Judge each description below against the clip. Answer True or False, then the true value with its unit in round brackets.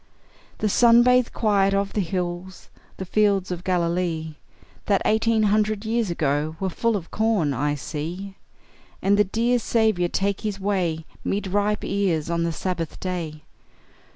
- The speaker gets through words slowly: False (155 wpm)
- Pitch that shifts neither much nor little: True (3.9 semitones)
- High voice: True (195 Hz)